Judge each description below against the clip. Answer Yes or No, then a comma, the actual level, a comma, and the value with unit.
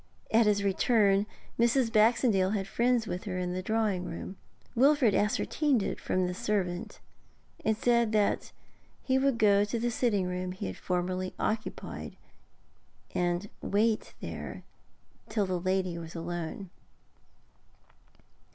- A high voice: Yes, high, 205 Hz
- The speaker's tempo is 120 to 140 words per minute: Yes, slow, 135 wpm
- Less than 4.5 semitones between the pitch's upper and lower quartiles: Yes, average, 3.8 semitones